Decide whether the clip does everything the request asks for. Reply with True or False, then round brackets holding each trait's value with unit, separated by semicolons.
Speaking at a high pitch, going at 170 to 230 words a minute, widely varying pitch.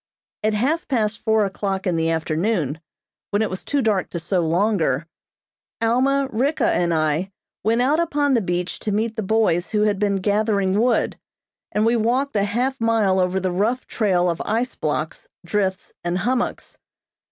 False (210 Hz; 175 wpm; 4.0 semitones)